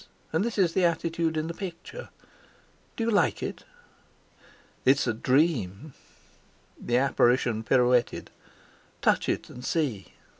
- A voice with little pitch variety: No, wide, 5.5 semitones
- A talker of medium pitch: Yes, medium, 150 Hz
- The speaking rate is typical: No, slow, 125 wpm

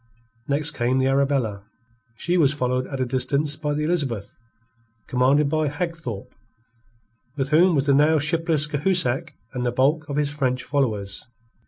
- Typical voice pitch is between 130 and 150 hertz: Yes, medium, 140 Hz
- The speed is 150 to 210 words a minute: Yes, average, 155 wpm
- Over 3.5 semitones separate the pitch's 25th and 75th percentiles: No, average, 3.1 semitones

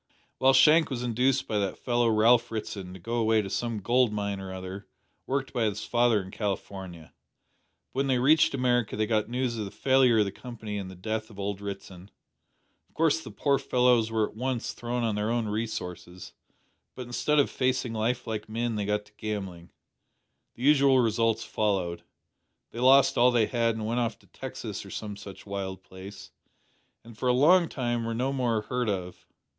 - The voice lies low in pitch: Yes, low, 115 Hz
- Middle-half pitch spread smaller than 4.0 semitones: Yes, average, 3.3 semitones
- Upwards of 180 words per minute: Yes, average, 195 wpm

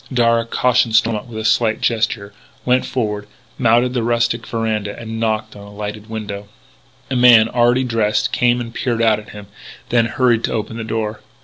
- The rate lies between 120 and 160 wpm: No, average, 185 wpm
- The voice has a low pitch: Yes, low, 115 Hz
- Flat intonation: Yes, narrow, 1.8 semitones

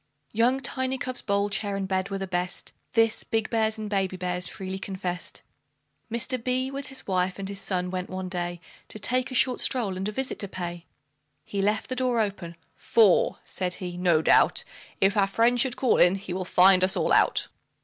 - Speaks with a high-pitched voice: Yes, high, 195 Hz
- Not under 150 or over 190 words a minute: No, fast, 205 wpm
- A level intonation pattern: No, average, 3.8 semitones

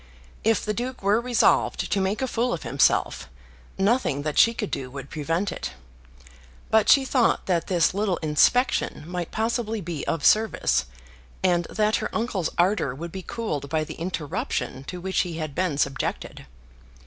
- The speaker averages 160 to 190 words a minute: Yes, average, 170 wpm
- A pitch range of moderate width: No, wide, 5.7 semitones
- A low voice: No, medium, 185 Hz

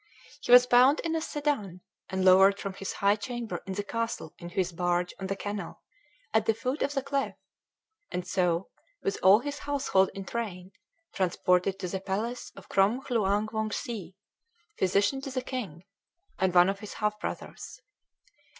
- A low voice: No, high, 200 Hz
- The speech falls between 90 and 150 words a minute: No, average, 170 wpm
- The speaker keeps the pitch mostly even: No, average, 4.3 semitones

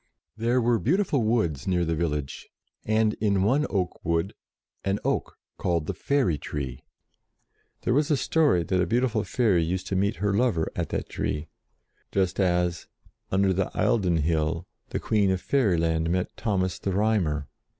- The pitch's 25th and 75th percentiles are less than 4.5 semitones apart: No, average, 4.8 semitones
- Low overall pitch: Yes, very low, 95 Hz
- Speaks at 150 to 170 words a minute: Yes, average, 160 wpm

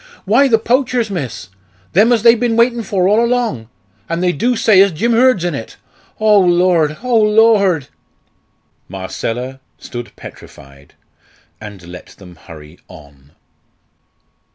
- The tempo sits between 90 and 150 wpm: Yes, slow, 135 wpm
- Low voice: No, medium, 185 Hz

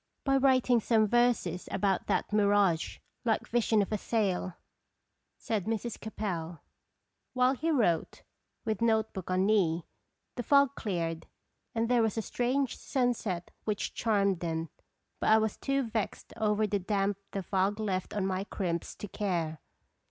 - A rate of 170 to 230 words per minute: No, average, 160 wpm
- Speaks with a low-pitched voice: No, high, 210 Hz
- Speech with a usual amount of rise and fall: Yes, average, 3.7 semitones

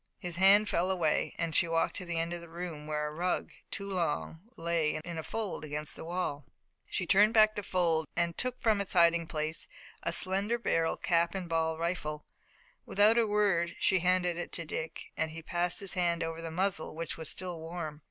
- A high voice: No, medium, 170 Hz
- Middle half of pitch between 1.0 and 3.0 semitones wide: Yes, narrow, 2.6 semitones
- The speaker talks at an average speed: No, fast, 210 wpm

